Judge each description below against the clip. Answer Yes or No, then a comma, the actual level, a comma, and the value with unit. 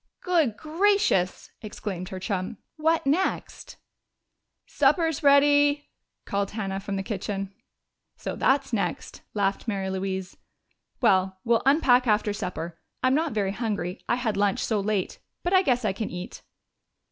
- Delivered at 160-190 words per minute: No, average, 140 wpm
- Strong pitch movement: Yes, wide, 6.5 semitones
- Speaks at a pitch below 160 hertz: No, high, 215 Hz